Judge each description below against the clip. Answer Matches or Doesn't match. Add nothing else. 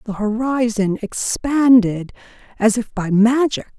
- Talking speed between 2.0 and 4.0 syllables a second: Matches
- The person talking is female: Matches